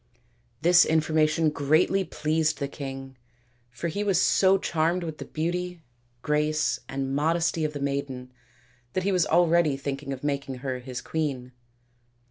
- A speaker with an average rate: Yes, average, 145 wpm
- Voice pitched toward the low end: No, medium, 155 Hz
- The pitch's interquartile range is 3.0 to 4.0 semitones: Yes, average, 3.4 semitones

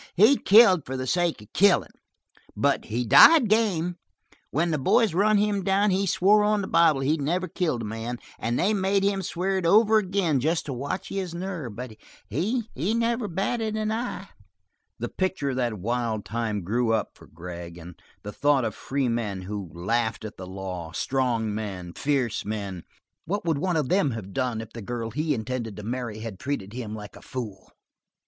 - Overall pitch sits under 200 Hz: Yes, low, 135 Hz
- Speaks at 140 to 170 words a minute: No, average, 195 wpm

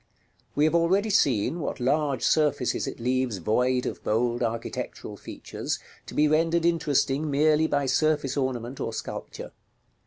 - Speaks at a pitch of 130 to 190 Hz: Yes, medium, 140 Hz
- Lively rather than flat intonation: No, average, 3.9 semitones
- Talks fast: No, average, 145 wpm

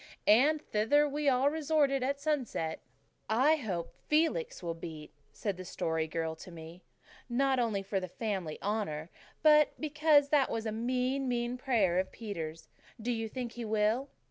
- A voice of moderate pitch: No, high, 235 Hz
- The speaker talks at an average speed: Yes, average, 165 wpm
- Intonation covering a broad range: Yes, wide, 7.1 semitones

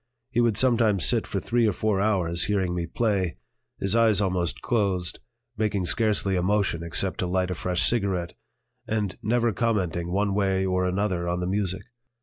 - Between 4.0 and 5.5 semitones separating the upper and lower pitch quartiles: No, average, 3.0 semitones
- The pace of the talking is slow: No, average, 175 wpm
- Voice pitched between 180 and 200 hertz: No, very low, 95 Hz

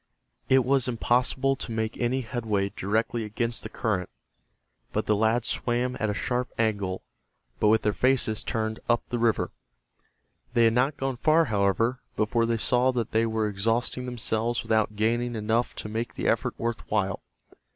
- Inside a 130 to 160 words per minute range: No, average, 170 wpm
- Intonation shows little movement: Yes, narrow, 2.1 semitones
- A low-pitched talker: Yes, low, 115 Hz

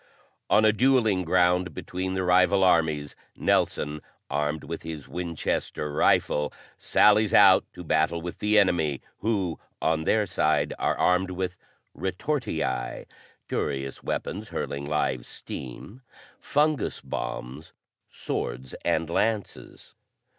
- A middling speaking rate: No, slow, 115 wpm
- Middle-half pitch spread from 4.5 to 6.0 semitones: Yes, average, 4.9 semitones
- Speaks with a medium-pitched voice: No, very low, 90 Hz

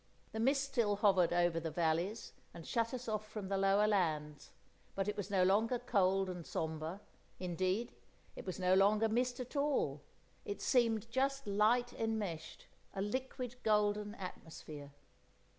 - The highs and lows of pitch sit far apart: No, average, 4.0 semitones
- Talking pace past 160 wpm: No, average, 155 wpm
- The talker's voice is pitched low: No, high, 205 Hz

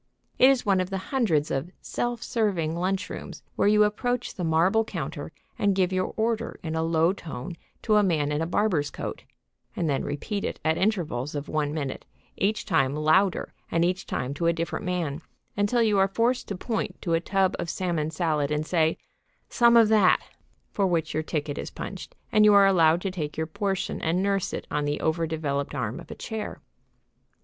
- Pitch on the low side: No, medium, 175 Hz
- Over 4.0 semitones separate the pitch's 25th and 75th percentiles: Yes, average, 4.4 semitones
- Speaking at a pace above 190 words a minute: Yes, average, 200 wpm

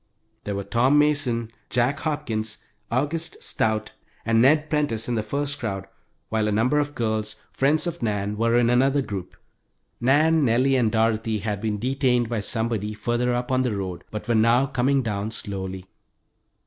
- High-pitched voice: No, low, 115 Hz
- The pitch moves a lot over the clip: No, average, 3.9 semitones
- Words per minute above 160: Yes, average, 170 wpm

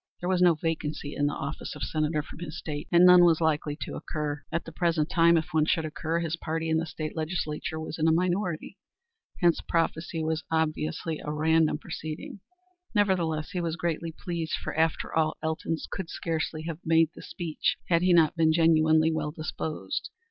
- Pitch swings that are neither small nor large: No, narrow, 1.4 semitones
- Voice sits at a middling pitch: Yes, medium, 160 Hz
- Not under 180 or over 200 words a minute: Yes, average, 190 wpm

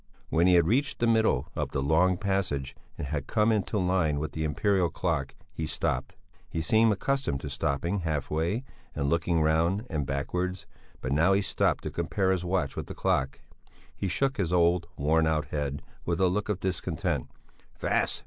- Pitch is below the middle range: Yes, very low, 85 Hz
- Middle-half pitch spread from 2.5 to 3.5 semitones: No, average, 4.0 semitones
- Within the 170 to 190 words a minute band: Yes, average, 185 wpm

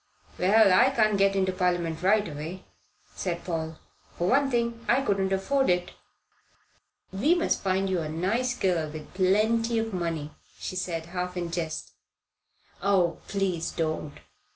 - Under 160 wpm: Yes, average, 150 wpm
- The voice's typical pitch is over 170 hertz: Yes, medium, 185 Hz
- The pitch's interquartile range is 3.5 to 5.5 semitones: Yes, average, 4.0 semitones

